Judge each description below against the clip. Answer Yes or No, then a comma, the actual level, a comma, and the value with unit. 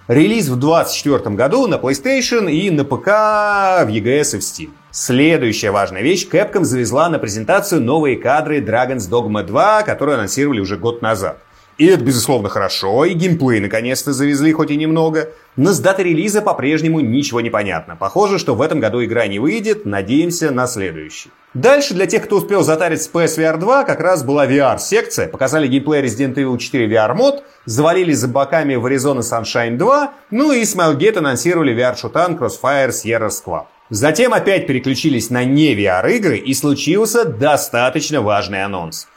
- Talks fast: Yes, fast, 165 wpm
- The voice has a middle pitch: Yes, medium, 145 Hz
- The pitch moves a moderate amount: No, wide, 6.2 semitones